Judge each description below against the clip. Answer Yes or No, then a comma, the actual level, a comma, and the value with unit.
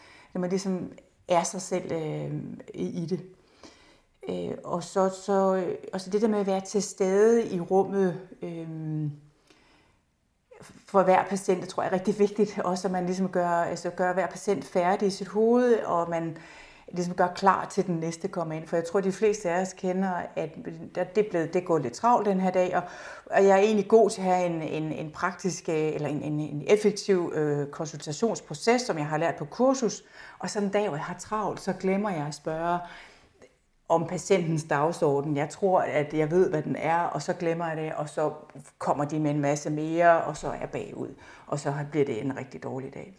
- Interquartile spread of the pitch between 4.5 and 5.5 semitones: No, average, 3.3 semitones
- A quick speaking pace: No, average, 210 wpm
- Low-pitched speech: No, medium, 180 Hz